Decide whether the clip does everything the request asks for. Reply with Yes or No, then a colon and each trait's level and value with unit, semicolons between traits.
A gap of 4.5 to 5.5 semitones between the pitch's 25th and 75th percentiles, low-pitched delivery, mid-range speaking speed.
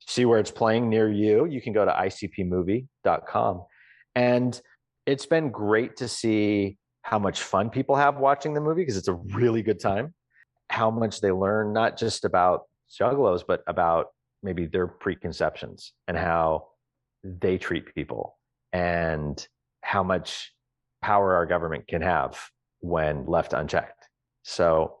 Yes: average, 5.1 semitones; low, 110 Hz; average, 145 wpm